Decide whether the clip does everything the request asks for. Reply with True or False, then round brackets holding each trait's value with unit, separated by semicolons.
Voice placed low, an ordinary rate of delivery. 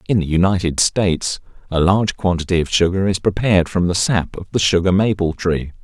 True (90 Hz; 195 wpm)